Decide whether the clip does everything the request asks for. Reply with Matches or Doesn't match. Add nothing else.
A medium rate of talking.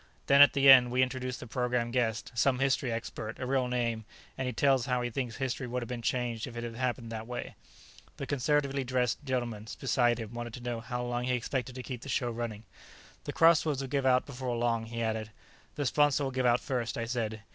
Doesn't match